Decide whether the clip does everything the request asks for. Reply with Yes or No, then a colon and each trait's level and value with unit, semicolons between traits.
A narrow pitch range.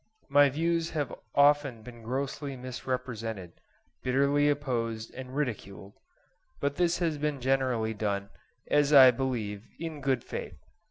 No: average, 4.0 semitones